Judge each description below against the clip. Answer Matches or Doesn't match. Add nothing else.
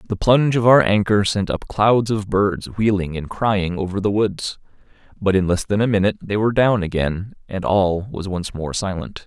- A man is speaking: Matches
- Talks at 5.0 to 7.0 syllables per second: Doesn't match